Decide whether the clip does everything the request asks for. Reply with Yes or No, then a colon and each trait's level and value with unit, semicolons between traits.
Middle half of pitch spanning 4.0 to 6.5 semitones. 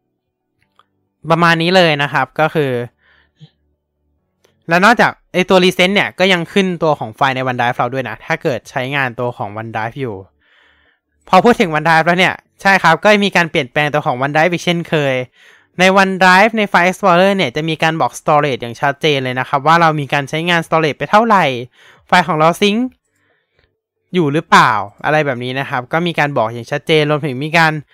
Yes: average, 5.1 semitones